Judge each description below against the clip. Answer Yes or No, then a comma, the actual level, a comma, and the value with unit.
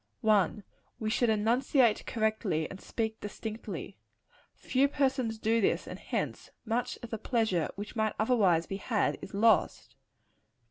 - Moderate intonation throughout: No, narrow, 2.1 semitones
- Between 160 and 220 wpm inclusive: No, average, 140 wpm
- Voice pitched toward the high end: Yes, high, 220 Hz